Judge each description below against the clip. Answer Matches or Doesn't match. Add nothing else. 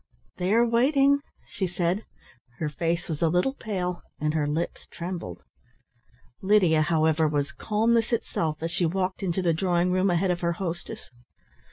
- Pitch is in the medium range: Matches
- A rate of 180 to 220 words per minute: Doesn't match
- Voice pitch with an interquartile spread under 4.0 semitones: Matches